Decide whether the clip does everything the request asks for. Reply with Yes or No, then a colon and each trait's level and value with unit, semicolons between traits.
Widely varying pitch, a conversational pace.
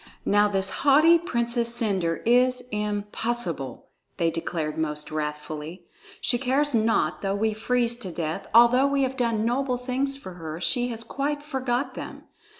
Yes: wide, 6.0 semitones; average, 150 wpm